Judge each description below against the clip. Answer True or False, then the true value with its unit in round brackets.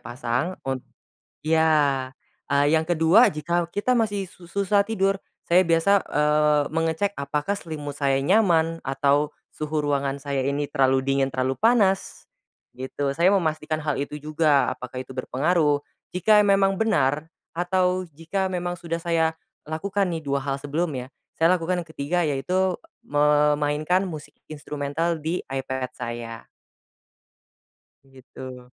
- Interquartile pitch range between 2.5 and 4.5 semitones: True (4.0 semitones)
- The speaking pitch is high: False (155 Hz)